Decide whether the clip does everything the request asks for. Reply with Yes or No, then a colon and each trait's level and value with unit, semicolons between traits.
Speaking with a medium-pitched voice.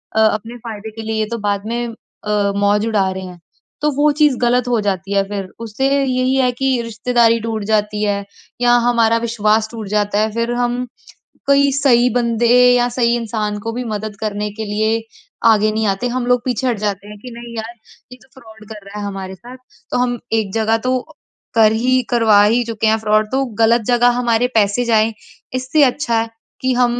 No: high, 225 Hz